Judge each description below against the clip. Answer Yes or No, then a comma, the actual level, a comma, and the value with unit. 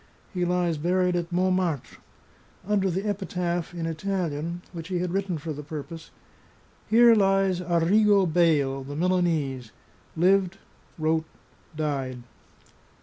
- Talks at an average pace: No, slow, 120 wpm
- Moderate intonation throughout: Yes, average, 3.0 semitones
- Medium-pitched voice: Yes, medium, 175 Hz